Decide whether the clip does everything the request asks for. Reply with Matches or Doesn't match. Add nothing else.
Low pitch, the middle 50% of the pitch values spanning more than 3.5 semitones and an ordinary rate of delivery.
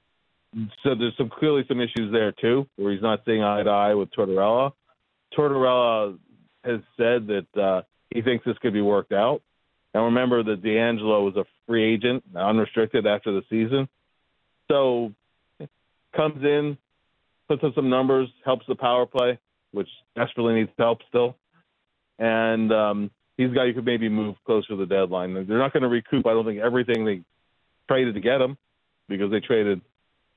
Doesn't match